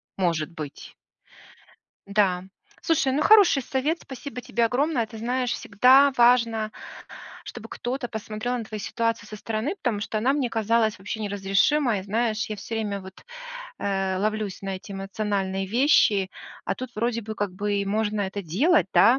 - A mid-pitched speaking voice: No, high, 220 Hz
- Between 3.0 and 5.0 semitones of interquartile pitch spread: Yes, average, 3.7 semitones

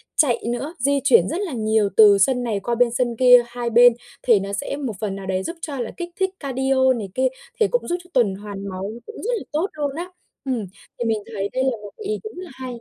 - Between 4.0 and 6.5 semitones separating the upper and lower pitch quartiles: Yes, average, 4.9 semitones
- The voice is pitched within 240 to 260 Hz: Yes, high, 245 Hz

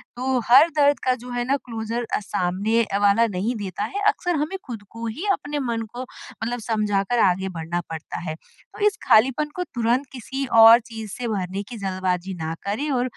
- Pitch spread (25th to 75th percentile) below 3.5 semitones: No, average, 4.3 semitones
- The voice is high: Yes, high, 230 Hz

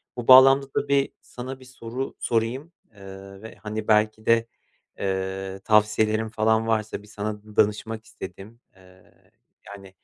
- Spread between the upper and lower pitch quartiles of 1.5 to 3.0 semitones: Yes, narrow, 2.5 semitones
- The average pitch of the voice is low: Yes, low, 110 Hz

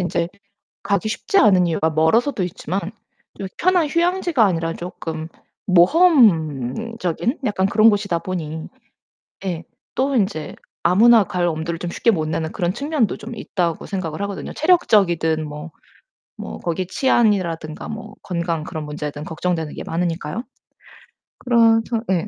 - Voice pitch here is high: No, medium, 180 Hz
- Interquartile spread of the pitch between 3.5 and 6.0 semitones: Yes, wide, 5.6 semitones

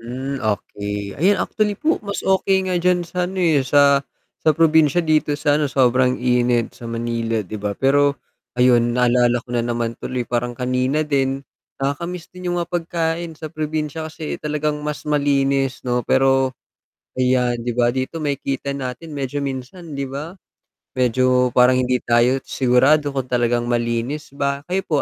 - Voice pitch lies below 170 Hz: Yes, low, 135 Hz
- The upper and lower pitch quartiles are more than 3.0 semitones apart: Yes, average, 3.8 semitones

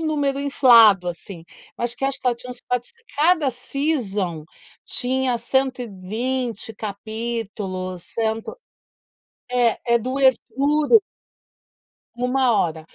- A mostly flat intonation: No, average, 3.9 semitones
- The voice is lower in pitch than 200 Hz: No, high, 245 Hz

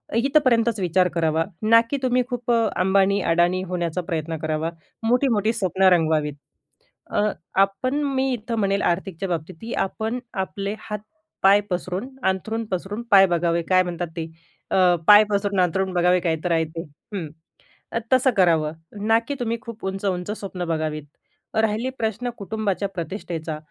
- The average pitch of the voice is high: Yes, high, 195 Hz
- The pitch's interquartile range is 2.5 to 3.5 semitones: No, average, 4.2 semitones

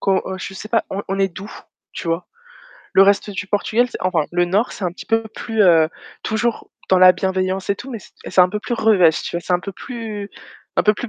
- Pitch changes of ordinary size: Yes, average, 3.1 semitones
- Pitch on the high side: Yes, high, 195 Hz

